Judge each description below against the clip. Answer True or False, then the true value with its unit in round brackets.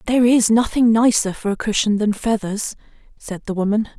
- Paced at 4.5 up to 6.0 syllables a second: True (5.4 syllables/s)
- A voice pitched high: True (215 Hz)